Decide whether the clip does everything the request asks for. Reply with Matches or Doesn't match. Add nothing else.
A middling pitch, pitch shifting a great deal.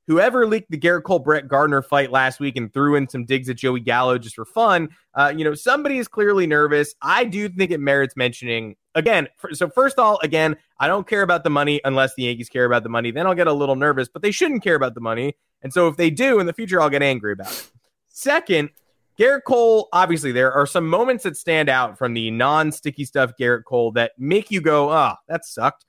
Matches